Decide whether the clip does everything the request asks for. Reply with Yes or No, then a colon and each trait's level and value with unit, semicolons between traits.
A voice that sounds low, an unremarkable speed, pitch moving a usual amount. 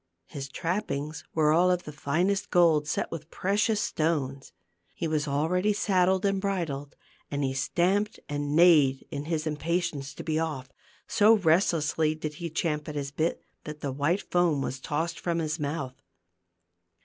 No: medium, 160 Hz; average, 165 wpm; average, 3.5 semitones